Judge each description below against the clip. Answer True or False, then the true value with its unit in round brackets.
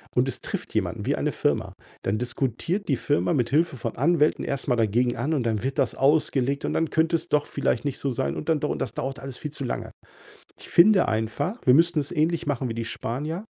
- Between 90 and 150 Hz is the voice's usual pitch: True (140 Hz)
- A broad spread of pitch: False (4.6 semitones)